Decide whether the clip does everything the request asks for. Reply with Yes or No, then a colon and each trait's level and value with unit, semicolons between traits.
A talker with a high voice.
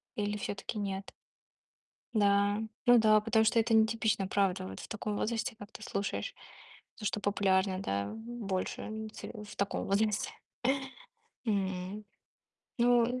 Yes: high, 205 Hz